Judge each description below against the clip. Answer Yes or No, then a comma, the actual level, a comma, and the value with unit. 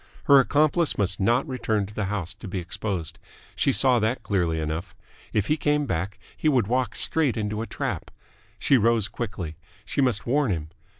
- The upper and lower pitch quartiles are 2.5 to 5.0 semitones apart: No, wide, 5.4 semitones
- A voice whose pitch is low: Yes, low, 110 Hz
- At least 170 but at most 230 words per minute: Yes, average, 185 wpm